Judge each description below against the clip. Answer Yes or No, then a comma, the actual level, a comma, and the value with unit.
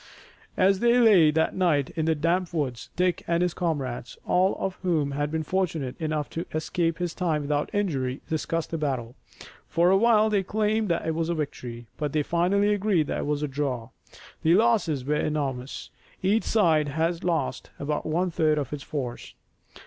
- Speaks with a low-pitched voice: No, medium, 160 Hz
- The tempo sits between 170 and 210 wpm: Yes, average, 185 wpm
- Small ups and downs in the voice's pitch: No, average, 3.9 semitones